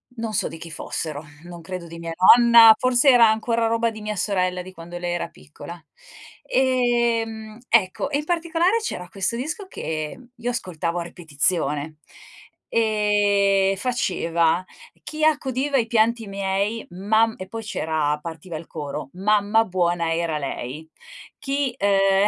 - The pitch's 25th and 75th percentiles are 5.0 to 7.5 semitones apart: Yes, wide, 5.4 semitones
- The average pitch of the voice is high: Yes, high, 200 Hz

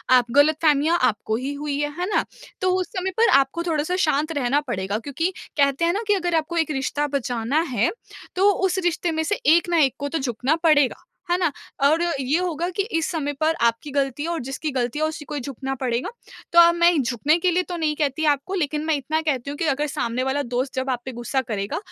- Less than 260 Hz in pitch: No, very high, 295 Hz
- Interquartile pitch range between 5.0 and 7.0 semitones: No, average, 4.1 semitones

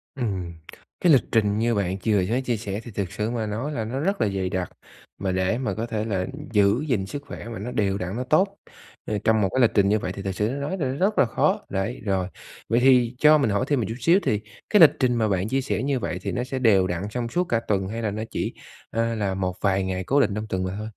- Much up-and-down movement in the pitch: No, average, 4.6 semitones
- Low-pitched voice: Yes, low, 110 Hz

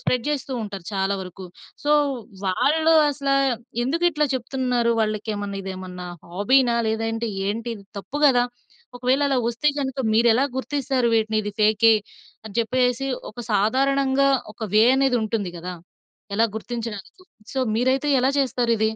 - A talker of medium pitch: No, high, 235 Hz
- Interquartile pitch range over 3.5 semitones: Yes, average, 4.1 semitones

